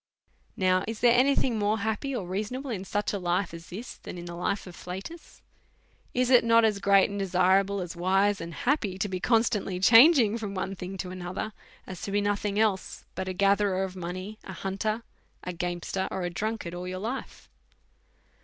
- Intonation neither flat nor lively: Yes, average, 3.0 semitones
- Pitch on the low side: No, high, 195 Hz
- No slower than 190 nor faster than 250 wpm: Yes, average, 200 wpm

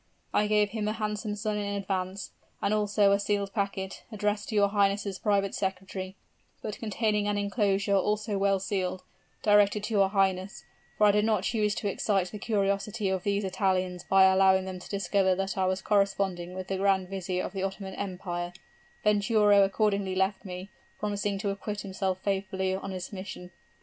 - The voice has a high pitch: Yes, high, 200 Hz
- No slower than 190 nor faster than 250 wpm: No, average, 180 wpm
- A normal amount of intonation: No, narrow, 1.5 semitones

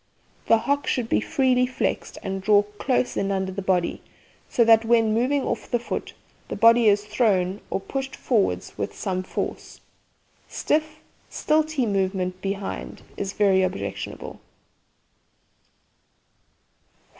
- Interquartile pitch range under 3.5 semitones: No, average, 4.6 semitones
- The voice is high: Yes, high, 210 Hz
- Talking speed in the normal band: No, slow, 130 wpm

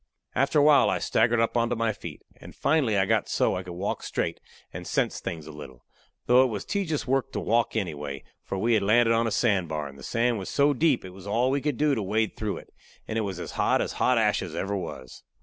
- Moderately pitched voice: No, low, 110 Hz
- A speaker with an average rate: No, fast, 250 wpm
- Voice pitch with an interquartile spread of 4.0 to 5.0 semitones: Yes, average, 4.7 semitones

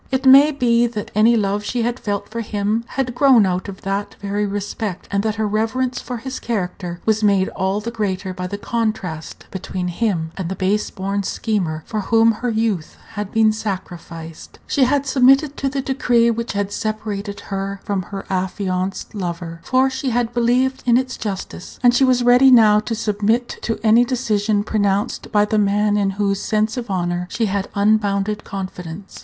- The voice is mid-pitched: No, high, 210 Hz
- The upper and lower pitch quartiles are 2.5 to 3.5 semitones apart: Yes, average, 3.2 semitones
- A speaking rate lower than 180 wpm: No, average, 185 wpm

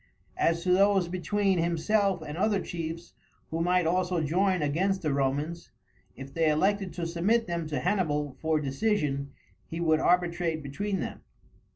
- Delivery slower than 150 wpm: No, average, 155 wpm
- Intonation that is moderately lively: Yes, average, 3.2 semitones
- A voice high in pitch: No, medium, 170 Hz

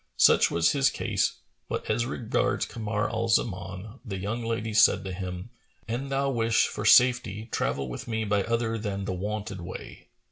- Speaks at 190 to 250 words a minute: No, average, 175 wpm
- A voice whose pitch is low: Yes, low, 110 Hz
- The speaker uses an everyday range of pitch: Yes, average, 3.1 semitones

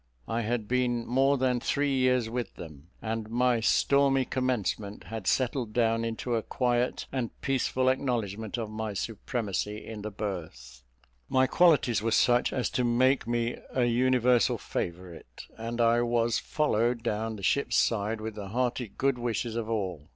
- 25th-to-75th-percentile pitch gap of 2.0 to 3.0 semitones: Yes, average, 2.7 semitones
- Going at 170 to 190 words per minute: No, average, 160 wpm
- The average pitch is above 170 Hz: No, low, 115 Hz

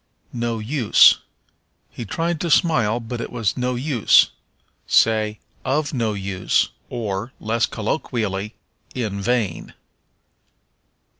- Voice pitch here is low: Yes, low, 115 Hz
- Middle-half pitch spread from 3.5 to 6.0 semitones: No, average, 3.0 semitones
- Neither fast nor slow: No, slow, 105 wpm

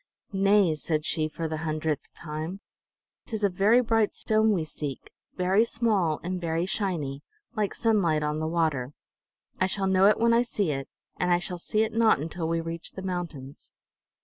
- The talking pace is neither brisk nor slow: Yes, average, 180 wpm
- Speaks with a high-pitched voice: No, medium, 180 Hz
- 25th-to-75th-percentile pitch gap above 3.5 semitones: Yes, average, 4.7 semitones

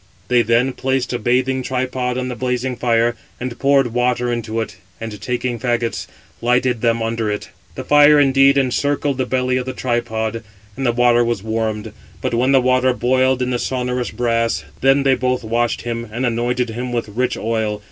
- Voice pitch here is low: Yes, low, 125 Hz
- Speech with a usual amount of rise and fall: No, narrow, 1.7 semitones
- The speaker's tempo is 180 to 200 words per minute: Yes, average, 190 wpm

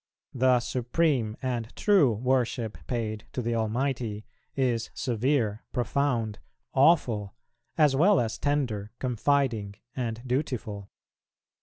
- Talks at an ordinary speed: No, slow, 105 wpm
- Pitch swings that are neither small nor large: Yes, average, 3.4 semitones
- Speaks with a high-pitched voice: No, low, 120 Hz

